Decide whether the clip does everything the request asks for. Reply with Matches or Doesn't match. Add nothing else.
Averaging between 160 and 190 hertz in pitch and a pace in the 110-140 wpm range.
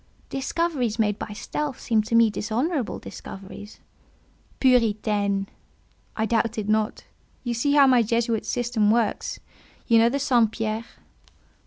Doesn't match